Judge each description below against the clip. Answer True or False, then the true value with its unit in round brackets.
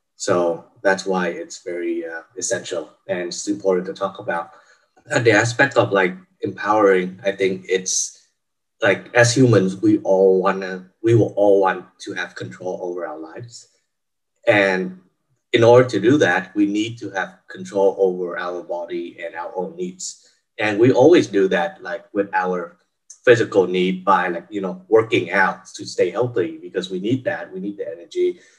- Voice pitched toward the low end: True (95 Hz)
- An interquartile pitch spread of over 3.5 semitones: True (4.6 semitones)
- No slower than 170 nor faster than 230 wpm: True (175 wpm)